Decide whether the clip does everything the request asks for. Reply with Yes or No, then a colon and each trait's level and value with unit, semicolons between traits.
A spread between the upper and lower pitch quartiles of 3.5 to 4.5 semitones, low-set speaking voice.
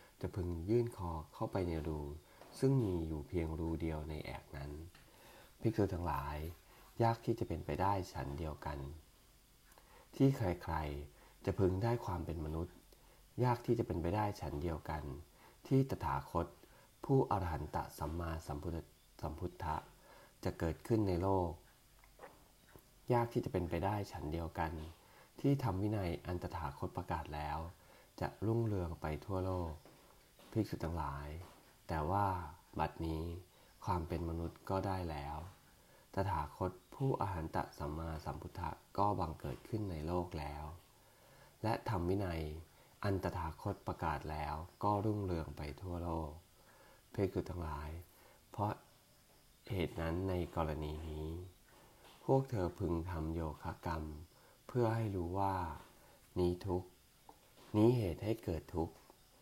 Yes: average, 3.8 semitones; very low, 85 Hz